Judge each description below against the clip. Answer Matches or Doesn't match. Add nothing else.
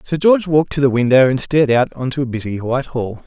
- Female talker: Doesn't match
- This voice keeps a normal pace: Doesn't match